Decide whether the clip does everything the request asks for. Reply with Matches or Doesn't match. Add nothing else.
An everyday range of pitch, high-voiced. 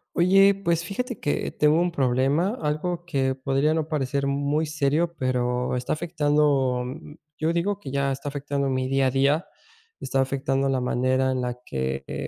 Doesn't match